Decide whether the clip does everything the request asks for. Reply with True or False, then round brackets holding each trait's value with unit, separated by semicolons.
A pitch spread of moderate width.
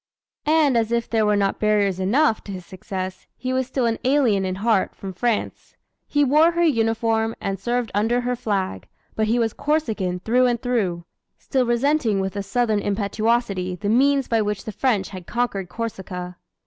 True (4.0 semitones)